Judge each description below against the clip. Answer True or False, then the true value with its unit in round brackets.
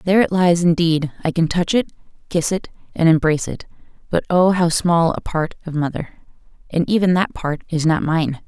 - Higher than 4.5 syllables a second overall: True (5.3 syllables/s)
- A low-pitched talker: False (170 Hz)